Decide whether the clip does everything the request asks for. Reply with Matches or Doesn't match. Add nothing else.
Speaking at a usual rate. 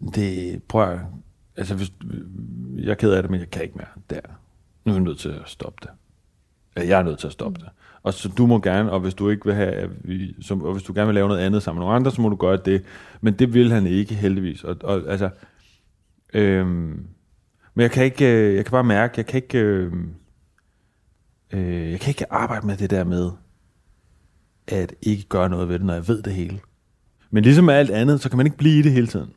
Doesn't match